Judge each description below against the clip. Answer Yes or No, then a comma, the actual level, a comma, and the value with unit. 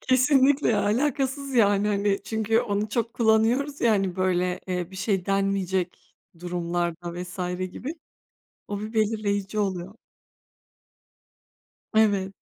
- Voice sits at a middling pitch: No, high, 205 Hz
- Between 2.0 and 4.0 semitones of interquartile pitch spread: Yes, average, 3.4 semitones